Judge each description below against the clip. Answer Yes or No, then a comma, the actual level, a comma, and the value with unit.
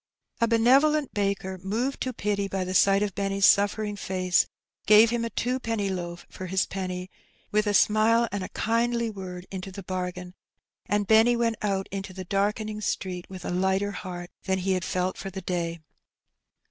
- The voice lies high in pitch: Yes, high, 195 Hz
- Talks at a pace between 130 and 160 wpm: No, average, 180 wpm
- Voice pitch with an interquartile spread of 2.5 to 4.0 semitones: Yes, average, 2.8 semitones